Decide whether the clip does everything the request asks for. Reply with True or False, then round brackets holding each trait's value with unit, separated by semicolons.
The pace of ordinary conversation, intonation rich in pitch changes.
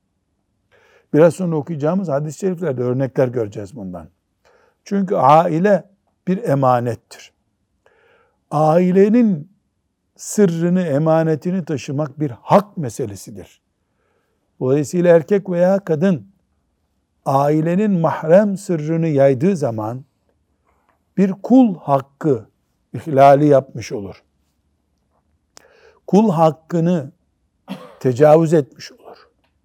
False (80 wpm; 8.5 semitones)